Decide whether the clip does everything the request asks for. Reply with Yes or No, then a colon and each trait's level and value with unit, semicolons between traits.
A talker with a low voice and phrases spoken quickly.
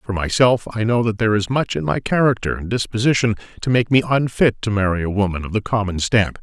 Yes: low, 110 Hz; fast, 235 wpm